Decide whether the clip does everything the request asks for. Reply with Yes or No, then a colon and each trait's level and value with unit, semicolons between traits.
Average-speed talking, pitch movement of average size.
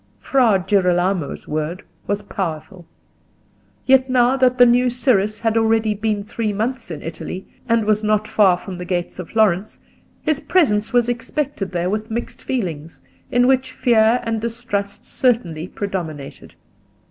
Yes: average, 145 wpm; average, 4.7 semitones